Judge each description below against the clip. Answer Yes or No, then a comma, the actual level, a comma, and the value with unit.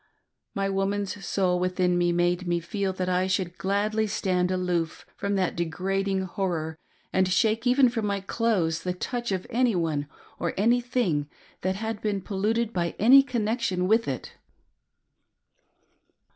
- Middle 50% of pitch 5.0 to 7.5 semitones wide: No, average, 3.3 semitones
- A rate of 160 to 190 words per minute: No, average, 145 wpm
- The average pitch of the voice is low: No, high, 190 Hz